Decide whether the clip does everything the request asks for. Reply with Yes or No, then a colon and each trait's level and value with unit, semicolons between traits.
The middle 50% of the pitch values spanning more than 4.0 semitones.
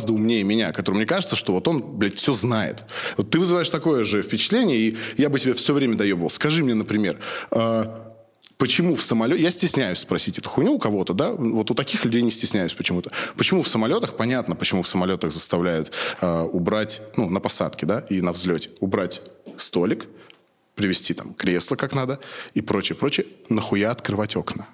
Yes: average, 4.4 semitones